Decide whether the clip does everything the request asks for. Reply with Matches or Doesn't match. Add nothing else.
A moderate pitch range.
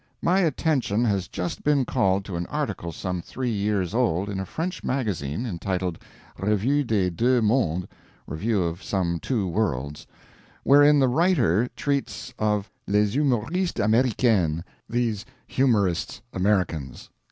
Doesn't match